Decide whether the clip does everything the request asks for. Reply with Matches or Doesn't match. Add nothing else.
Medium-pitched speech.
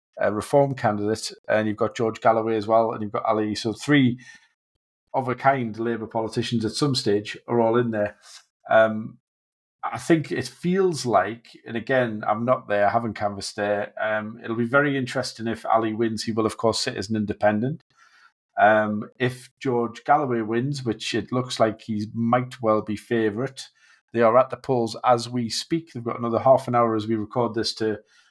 Doesn't match